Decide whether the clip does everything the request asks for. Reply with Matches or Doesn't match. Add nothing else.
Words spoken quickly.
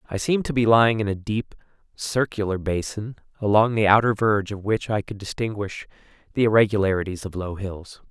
Doesn't match